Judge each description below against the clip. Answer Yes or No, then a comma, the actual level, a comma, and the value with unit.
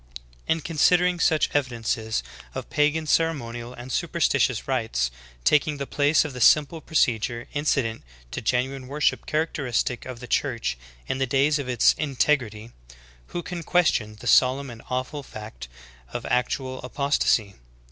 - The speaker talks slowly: No, average, 150 wpm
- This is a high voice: No, low, 130 Hz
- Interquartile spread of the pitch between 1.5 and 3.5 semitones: No, average, 4.1 semitones